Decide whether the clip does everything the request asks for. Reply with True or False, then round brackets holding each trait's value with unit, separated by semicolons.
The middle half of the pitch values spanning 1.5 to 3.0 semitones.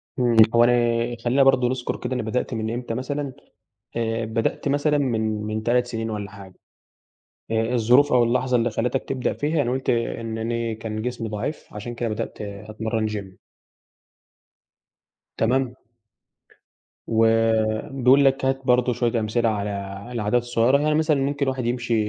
True (2.5 semitones)